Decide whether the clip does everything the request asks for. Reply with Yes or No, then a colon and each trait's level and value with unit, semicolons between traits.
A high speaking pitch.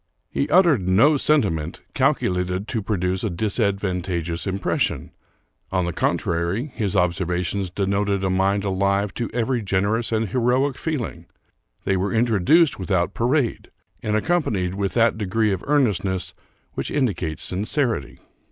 No: low, 100 Hz